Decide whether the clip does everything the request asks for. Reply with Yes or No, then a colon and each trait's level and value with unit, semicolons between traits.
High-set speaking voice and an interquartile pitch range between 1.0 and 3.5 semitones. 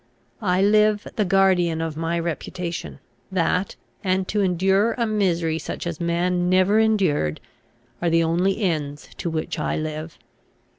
No: medium, 180 Hz; average, 2.8 semitones